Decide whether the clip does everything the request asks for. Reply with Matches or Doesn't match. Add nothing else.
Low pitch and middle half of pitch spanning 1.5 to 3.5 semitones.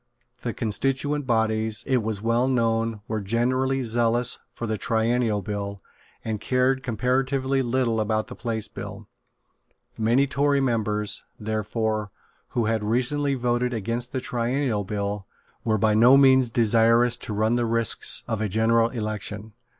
Matches